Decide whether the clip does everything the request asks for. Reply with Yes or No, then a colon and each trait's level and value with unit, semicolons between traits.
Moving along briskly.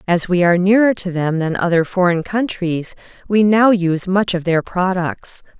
No: average, 180 wpm